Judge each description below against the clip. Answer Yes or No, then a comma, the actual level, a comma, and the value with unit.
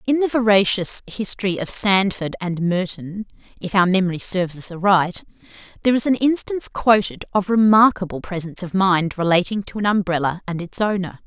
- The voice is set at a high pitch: Yes, high, 195 Hz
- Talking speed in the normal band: Yes, average, 165 wpm